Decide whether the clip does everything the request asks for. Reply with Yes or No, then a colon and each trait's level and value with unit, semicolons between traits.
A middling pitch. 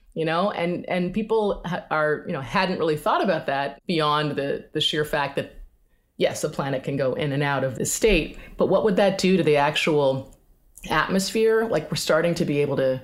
Yes: medium, 155 Hz